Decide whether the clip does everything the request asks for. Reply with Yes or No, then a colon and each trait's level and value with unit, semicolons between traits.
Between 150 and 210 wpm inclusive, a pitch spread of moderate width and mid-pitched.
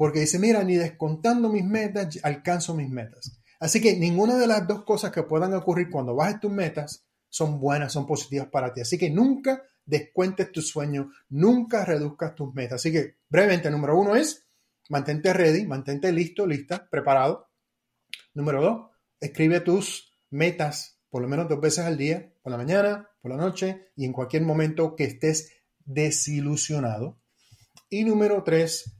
Yes: average, 165 wpm; average, 4.6 semitones; medium, 160 Hz